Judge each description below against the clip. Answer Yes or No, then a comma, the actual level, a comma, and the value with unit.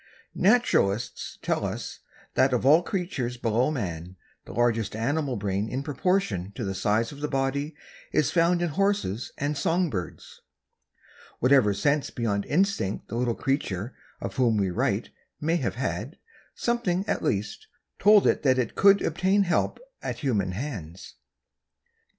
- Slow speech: No, average, 150 wpm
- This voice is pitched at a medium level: No, low, 130 Hz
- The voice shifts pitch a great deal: Yes, wide, 7.9 semitones